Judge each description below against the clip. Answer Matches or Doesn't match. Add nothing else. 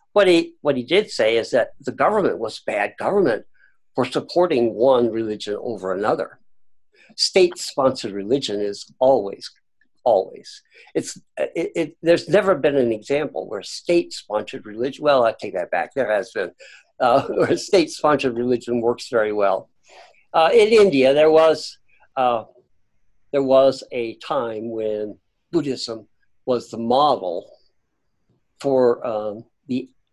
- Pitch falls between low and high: Doesn't match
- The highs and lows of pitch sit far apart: Matches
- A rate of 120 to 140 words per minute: Matches